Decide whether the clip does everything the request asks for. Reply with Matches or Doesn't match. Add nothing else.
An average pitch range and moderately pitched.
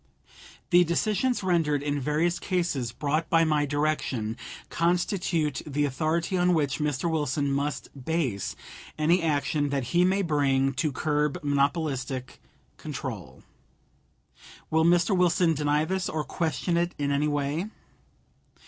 Matches